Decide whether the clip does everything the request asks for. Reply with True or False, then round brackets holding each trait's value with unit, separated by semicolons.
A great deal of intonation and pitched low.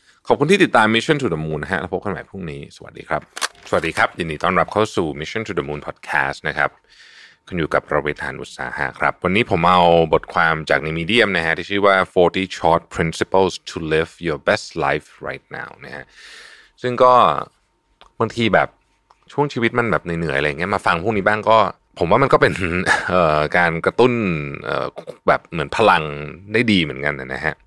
True (5.8 semitones; 90 Hz)